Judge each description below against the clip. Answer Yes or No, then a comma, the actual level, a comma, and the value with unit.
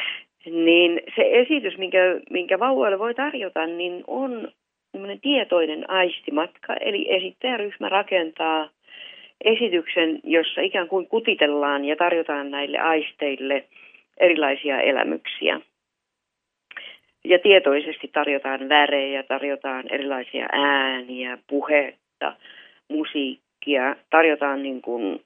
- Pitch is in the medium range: Yes, medium, 160 Hz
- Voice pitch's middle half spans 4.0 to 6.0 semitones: Yes, average, 5.0 semitones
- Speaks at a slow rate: Yes, slow, 90 wpm